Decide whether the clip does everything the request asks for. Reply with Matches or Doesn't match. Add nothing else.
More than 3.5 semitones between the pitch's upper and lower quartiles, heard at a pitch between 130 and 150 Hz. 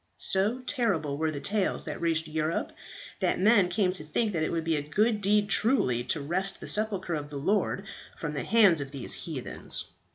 Doesn't match